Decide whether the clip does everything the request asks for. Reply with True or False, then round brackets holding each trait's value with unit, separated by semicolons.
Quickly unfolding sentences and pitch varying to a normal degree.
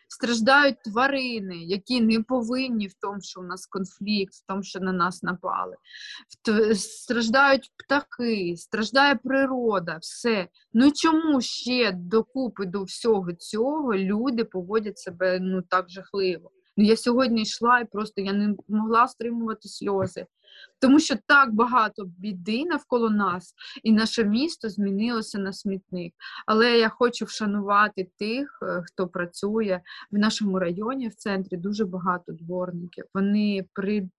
False (135 wpm; 4.1 semitones)